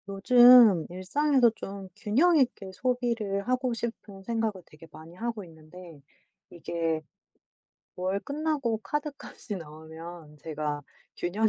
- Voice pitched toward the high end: Yes, high, 200 Hz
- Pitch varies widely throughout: Yes, wide, 6.3 semitones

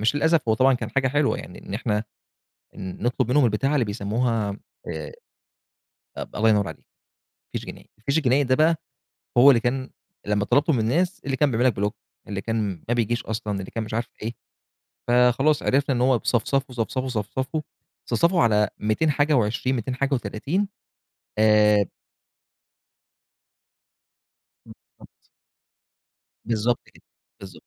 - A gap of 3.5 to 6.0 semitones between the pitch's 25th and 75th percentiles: Yes, average, 4.2 semitones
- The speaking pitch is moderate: No, low, 120 Hz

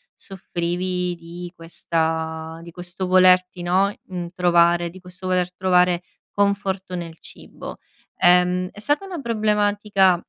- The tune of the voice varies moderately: No, narrow, 1.7 semitones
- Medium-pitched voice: Yes, medium, 180 Hz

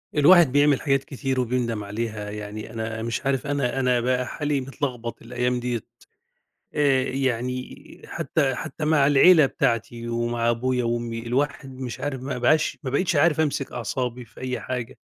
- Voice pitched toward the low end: Yes, low, 125 Hz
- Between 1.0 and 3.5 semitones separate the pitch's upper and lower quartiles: Yes, average, 2.9 semitones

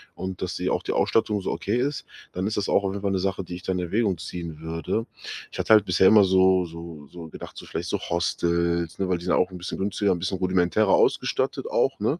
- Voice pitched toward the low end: Yes, very low, 95 Hz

